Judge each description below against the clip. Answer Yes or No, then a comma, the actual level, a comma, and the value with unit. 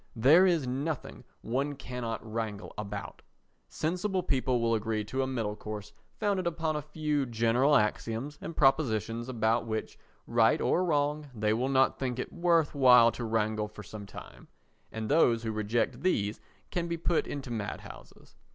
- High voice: No, low, 125 Hz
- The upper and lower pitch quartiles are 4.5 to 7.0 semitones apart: Yes, average, 5.2 semitones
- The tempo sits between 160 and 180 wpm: Yes, average, 165 wpm